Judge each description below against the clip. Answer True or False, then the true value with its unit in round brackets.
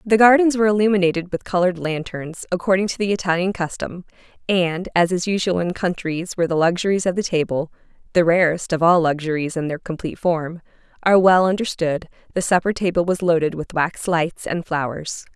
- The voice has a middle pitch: True (175 Hz)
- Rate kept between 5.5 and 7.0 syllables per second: True (5.8 syllables/s)